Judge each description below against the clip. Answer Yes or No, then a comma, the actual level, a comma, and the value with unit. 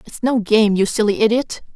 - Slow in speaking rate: No, fast, 205 wpm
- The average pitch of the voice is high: Yes, high, 220 Hz